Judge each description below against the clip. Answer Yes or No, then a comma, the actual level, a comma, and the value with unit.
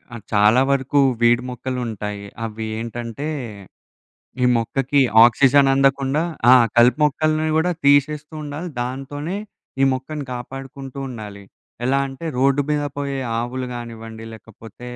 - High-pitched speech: No, low, 130 Hz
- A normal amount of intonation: Yes, average, 3.3 semitones